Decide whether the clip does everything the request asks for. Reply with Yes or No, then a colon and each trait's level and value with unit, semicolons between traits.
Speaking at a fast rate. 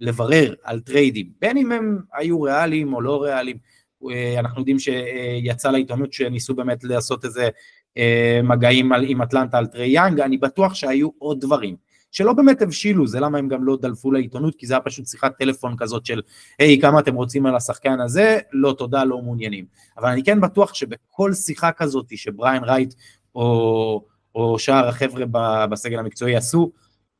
Yes: fast, 165 wpm